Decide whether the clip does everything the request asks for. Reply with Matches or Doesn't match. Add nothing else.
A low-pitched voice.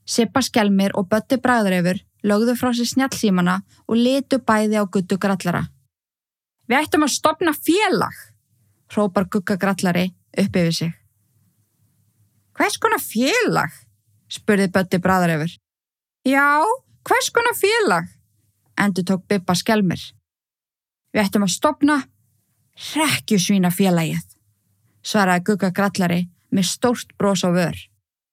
Doesn't match